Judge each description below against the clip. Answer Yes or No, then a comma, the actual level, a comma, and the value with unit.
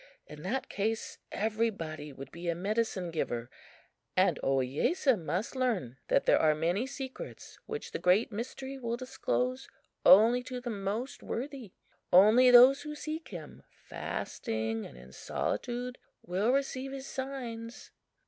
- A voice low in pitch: No, high, 230 Hz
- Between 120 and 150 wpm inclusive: Yes, average, 140 wpm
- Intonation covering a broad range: Yes, wide, 6.9 semitones